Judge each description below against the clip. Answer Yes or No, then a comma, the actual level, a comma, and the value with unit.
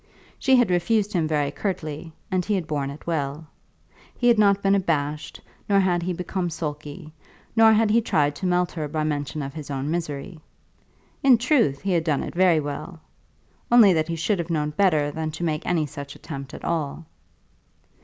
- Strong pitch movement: No, average, 4.2 semitones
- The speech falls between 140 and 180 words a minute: No, average, 195 wpm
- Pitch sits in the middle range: Yes, medium, 165 Hz